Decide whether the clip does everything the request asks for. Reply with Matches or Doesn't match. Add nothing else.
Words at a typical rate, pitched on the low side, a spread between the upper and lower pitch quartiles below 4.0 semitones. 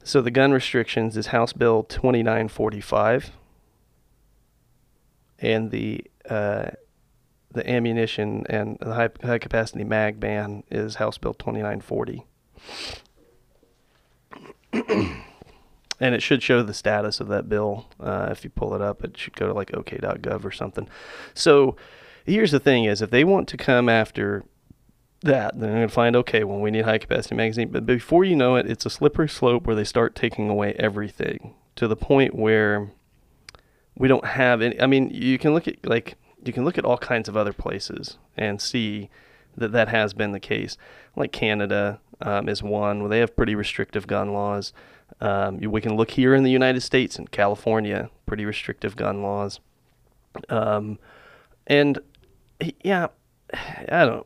Matches